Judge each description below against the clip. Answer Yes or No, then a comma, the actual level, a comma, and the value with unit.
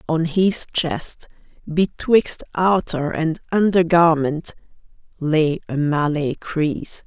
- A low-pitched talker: No, medium, 160 Hz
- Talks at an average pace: No, slow, 100 wpm